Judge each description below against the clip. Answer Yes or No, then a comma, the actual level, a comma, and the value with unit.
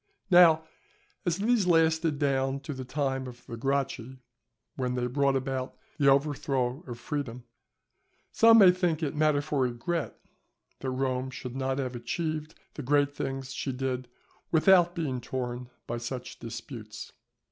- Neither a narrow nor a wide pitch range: Yes, average, 3.4 semitones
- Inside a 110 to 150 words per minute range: Yes, average, 145 wpm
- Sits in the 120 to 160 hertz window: Yes, low, 135 Hz